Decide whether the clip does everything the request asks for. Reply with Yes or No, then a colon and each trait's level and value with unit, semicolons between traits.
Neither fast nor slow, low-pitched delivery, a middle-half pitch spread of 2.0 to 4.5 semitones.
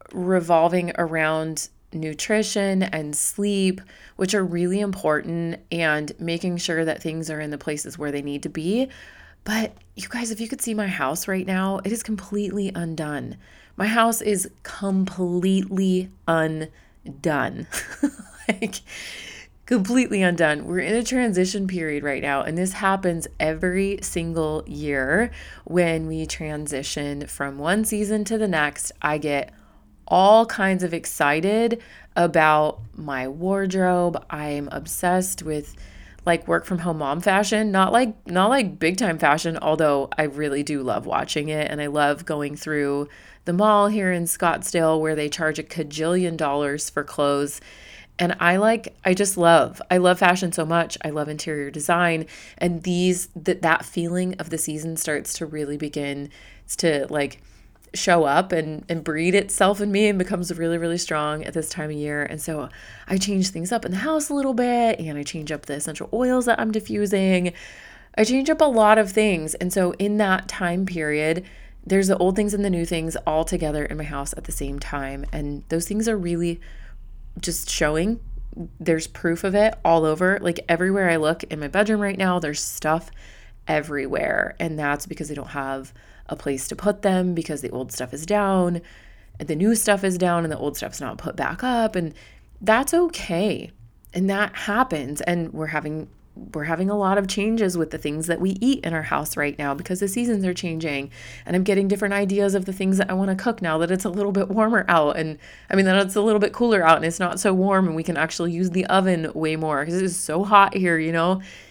No: average, 190 wpm; medium, 175 Hz; average, 4.2 semitones